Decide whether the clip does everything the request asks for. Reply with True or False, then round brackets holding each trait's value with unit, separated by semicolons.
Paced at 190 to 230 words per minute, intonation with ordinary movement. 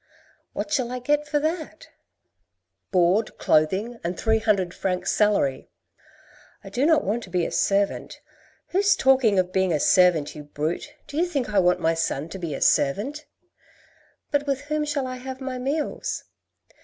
False (195 wpm; 7.8 semitones)